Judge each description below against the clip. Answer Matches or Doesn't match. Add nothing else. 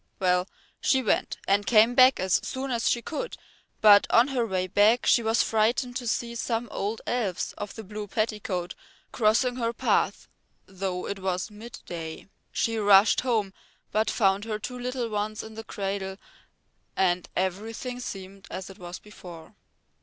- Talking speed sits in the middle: Matches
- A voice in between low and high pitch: Doesn't match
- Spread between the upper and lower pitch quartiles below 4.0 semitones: Matches